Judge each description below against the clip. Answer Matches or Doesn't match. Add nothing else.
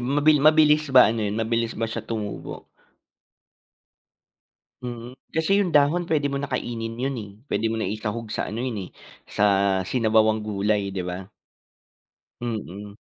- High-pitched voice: Doesn't match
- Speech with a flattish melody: Doesn't match